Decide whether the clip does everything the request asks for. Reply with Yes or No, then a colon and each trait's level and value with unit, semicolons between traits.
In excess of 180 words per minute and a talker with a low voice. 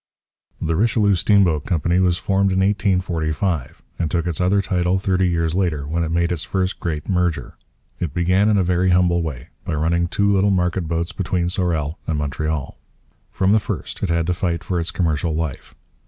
Yes: average, 190 wpm; very low, 85 Hz